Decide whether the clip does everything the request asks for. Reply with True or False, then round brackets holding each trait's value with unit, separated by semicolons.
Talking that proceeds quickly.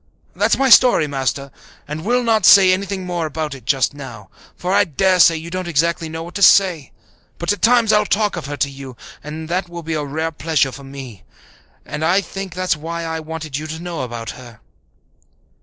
True (210 wpm)